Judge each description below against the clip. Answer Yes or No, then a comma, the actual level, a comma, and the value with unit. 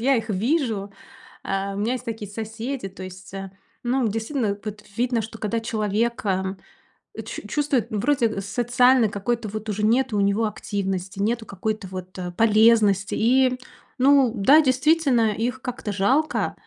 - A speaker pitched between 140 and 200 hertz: No, high, 220 Hz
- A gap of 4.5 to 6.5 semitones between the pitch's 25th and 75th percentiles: No, average, 3.7 semitones